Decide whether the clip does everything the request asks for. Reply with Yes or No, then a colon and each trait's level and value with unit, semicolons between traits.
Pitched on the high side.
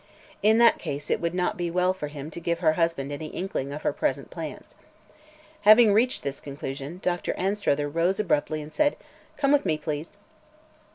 No: medium, 170 Hz